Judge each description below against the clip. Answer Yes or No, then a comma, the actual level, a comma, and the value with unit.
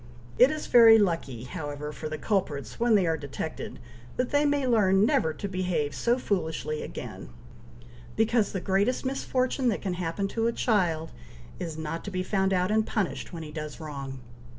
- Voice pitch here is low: No, medium, 185 Hz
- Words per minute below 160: No, average, 180 wpm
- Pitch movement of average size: No, wide, 6.0 semitones